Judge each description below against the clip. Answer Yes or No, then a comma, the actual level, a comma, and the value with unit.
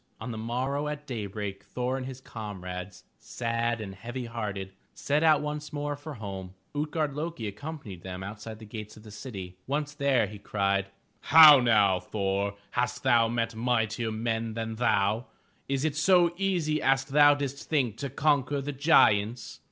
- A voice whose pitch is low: Yes, low, 120 Hz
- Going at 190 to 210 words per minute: No, average, 165 wpm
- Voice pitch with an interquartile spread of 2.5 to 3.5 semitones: No, wide, 5.5 semitones